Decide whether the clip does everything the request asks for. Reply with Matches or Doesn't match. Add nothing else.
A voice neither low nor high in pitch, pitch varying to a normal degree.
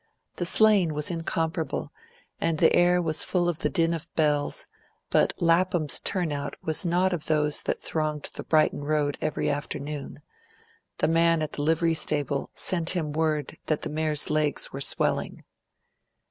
Doesn't match